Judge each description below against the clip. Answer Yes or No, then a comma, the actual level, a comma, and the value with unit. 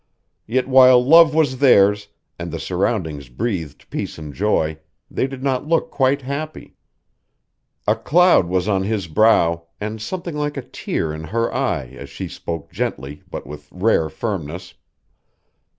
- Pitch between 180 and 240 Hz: No, low, 105 Hz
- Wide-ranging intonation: Yes, wide, 8.3 semitones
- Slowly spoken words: No, average, 150 wpm